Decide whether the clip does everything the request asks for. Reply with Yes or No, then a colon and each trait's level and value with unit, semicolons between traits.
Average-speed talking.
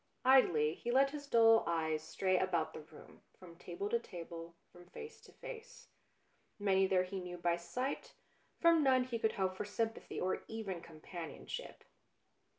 Yes: average, 165 wpm